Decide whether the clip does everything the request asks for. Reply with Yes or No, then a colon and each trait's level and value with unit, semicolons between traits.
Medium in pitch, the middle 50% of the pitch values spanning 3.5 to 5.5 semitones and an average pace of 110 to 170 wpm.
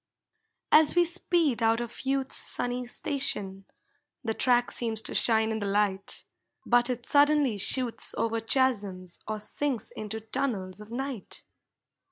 No: high, 235 Hz; average, 4.0 semitones; average, 140 wpm